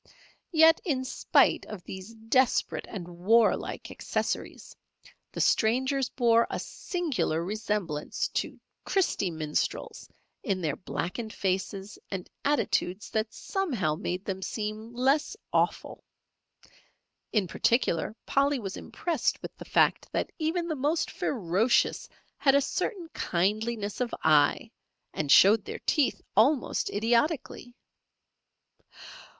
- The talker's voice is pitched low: No, high, 225 Hz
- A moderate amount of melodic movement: No, wide, 6.3 semitones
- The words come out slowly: Yes, slow, 115 wpm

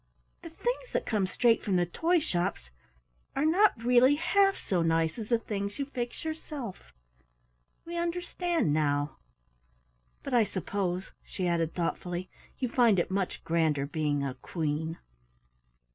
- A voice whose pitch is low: No, high, 200 Hz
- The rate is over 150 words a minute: No, average, 145 wpm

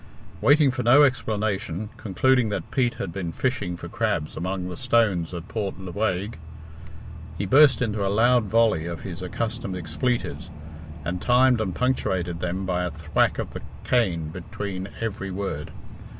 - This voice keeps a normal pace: Yes, average, 155 wpm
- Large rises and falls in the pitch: No, average, 5.0 semitones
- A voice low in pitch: Yes, low, 100 Hz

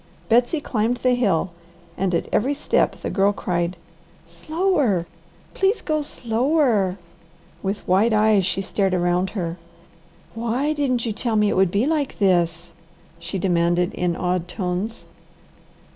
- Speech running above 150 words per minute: No, average, 140 wpm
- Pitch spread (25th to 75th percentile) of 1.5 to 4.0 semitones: No, wide, 5.5 semitones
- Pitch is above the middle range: Yes, high, 200 Hz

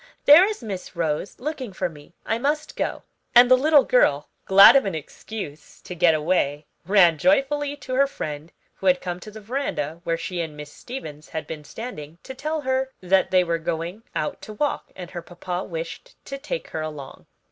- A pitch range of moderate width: No, wide, 8.4 semitones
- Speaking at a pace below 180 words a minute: No, average, 200 wpm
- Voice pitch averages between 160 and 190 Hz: Yes, medium, 185 Hz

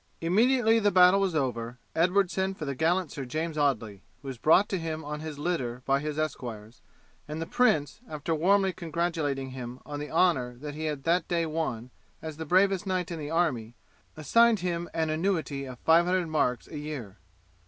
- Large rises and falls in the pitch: No, average, 4.5 semitones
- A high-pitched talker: No, medium, 155 Hz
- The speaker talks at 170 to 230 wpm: Yes, average, 195 wpm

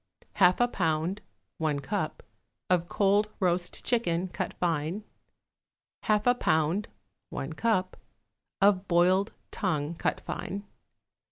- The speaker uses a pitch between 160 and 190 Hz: Yes, medium, 185 Hz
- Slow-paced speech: Yes, slow, 110 wpm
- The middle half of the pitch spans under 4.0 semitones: Yes, average, 3.6 semitones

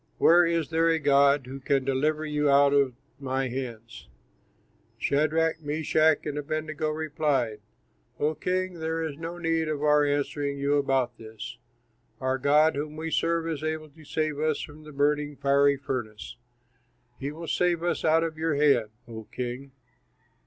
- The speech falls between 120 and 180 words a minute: Yes, average, 160 wpm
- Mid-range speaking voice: Yes, medium, 150 Hz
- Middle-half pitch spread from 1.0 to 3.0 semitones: Yes, narrow, 2.4 semitones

